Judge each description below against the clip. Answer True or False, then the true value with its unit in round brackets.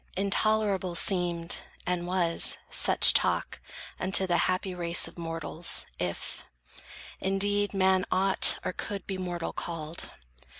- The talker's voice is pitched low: False (185 Hz)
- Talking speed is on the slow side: True (120 wpm)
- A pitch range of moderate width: False (2.2 semitones)